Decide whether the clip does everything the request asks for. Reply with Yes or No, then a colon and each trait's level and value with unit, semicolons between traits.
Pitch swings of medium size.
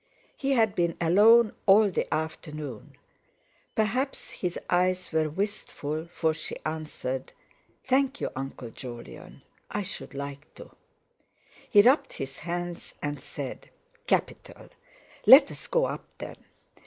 No: wide, 6.0 semitones